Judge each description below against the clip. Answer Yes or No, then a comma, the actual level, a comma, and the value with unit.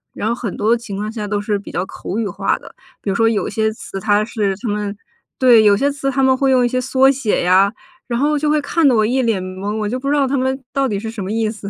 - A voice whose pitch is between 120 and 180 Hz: No, high, 225 Hz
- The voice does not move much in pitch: No, average, 4.2 semitones